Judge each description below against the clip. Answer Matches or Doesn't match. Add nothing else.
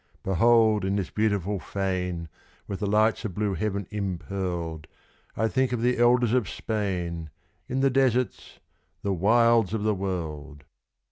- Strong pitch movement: Doesn't match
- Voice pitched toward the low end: Matches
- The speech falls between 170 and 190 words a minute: Doesn't match